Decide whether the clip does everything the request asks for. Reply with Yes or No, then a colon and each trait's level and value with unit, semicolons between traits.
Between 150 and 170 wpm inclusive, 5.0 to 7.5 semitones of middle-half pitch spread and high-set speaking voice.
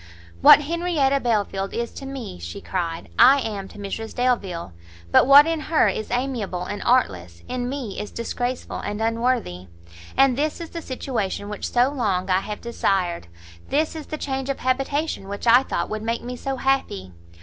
No: average, 180 wpm; wide, 5.5 semitones; high, 240 Hz